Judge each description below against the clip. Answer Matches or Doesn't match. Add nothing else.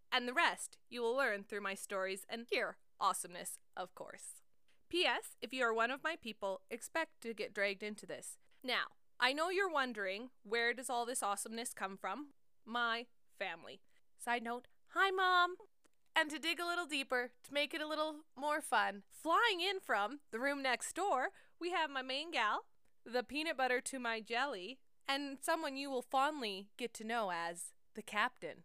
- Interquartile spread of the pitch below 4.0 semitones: Doesn't match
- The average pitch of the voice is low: Doesn't match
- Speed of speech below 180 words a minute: Doesn't match